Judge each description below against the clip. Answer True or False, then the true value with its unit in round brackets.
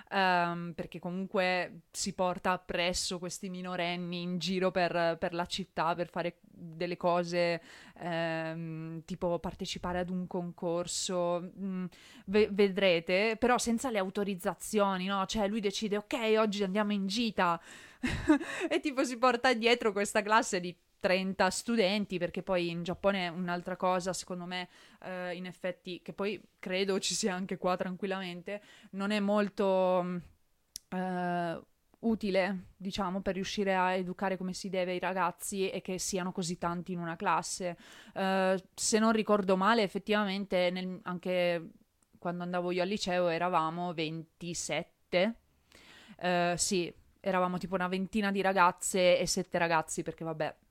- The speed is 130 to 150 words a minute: True (145 wpm)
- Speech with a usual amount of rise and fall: False (2.1 semitones)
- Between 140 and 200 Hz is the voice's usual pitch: True (185 Hz)